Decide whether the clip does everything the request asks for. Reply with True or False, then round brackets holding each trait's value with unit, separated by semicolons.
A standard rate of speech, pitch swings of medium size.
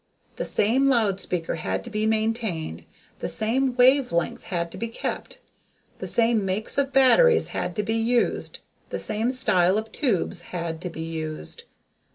False (170 wpm; 5.7 semitones)